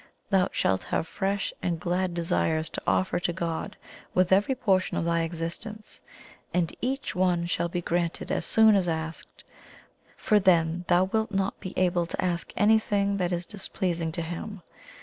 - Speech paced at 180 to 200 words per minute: No, average, 170 wpm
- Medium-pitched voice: Yes, medium, 180 Hz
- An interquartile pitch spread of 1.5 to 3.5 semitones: Yes, average, 2.8 semitones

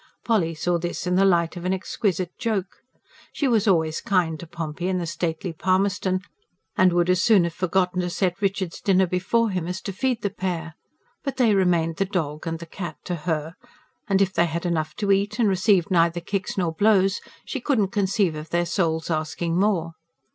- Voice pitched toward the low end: No, medium, 180 Hz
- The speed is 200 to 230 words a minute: Yes, fast, 205 wpm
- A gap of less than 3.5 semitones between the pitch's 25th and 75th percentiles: Yes, average, 2.7 semitones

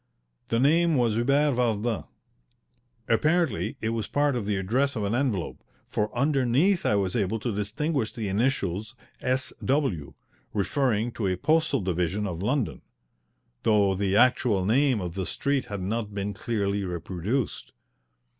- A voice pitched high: No, low, 110 Hz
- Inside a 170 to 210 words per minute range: No, average, 145 wpm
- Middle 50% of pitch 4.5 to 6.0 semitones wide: Yes, average, 5.1 semitones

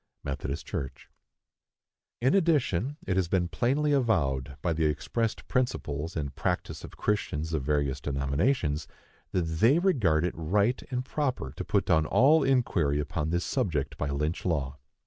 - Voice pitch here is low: Yes, very low, 85 Hz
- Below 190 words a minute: Yes, average, 150 wpm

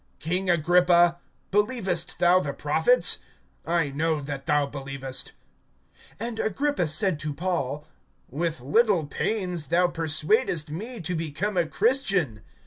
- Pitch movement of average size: Yes, average, 4.4 semitones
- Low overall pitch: No, medium, 170 Hz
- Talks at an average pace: No, slow, 125 wpm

